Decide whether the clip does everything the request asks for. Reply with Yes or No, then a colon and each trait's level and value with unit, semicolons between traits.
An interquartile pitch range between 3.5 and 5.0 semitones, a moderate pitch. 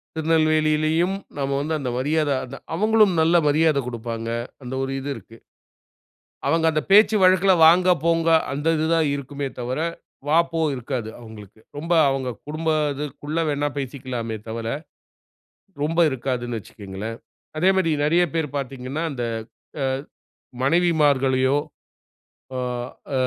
Yes: average, 4.2 semitones; medium, 145 Hz